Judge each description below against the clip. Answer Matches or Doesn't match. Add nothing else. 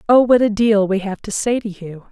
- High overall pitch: Matches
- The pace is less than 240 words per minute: Doesn't match